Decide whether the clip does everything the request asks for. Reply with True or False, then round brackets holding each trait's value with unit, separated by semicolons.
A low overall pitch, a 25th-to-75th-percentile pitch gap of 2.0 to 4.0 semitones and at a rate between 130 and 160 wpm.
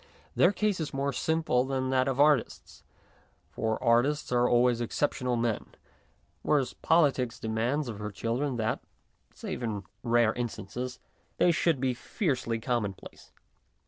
True (125 Hz; 3.4 semitones; 140 wpm)